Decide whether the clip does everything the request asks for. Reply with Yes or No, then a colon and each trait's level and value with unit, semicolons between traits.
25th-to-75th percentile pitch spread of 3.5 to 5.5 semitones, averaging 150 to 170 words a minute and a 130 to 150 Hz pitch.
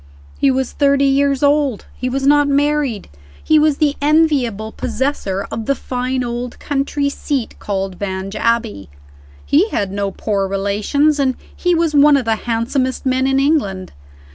No: average, 4.7 semitones; average, 160 wpm; very high, 265 Hz